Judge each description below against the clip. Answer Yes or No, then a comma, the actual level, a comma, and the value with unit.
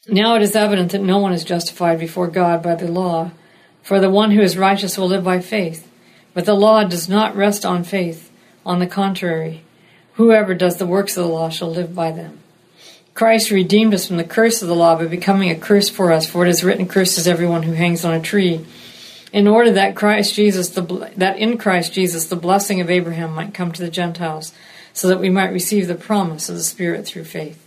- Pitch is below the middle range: No, medium, 180 Hz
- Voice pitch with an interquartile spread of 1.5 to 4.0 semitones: Yes, average, 2.7 semitones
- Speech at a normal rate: No, fast, 225 wpm